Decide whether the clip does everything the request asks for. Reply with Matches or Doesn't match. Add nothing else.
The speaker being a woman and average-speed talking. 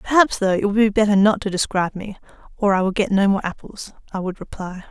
Doesn't match